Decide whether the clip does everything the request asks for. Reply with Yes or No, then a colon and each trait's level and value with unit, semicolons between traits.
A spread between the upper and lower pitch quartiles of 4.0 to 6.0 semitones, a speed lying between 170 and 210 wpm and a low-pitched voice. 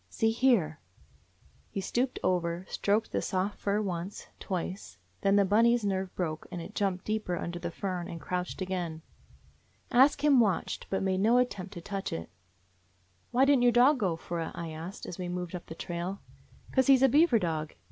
No: average, 4.5 semitones; fast, 205 wpm; high, 190 Hz